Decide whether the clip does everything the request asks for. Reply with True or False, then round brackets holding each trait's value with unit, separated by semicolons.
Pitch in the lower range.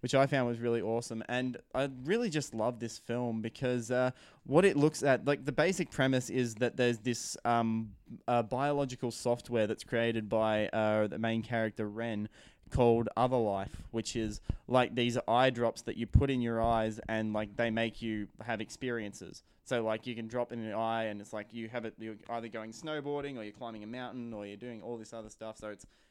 True (115 Hz)